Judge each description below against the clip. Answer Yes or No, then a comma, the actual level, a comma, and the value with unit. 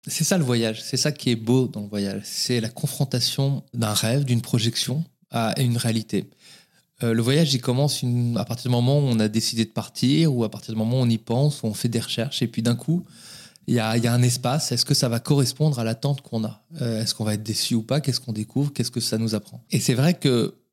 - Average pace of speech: No, fast, 265 wpm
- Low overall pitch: Yes, low, 120 Hz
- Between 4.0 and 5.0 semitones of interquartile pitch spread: No, average, 3.5 semitones